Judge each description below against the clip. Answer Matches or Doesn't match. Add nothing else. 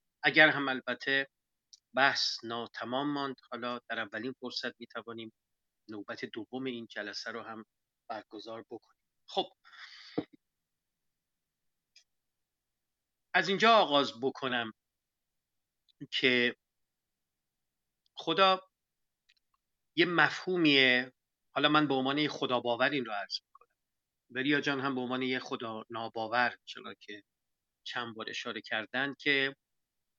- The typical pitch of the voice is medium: Doesn't match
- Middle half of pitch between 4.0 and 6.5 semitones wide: Doesn't match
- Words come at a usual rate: Doesn't match